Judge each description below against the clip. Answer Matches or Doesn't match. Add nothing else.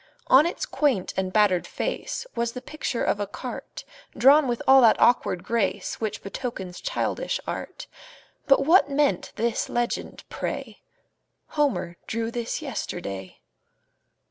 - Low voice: Doesn't match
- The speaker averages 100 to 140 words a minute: Matches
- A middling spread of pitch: Doesn't match